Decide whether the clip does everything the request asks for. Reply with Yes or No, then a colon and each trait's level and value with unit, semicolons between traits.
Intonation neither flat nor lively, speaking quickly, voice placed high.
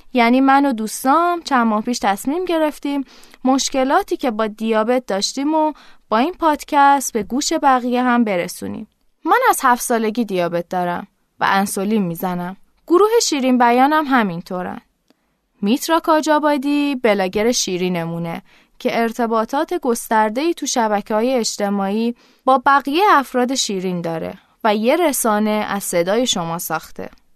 No: average, 5.0 semitones; average, 130 wpm; high, 245 Hz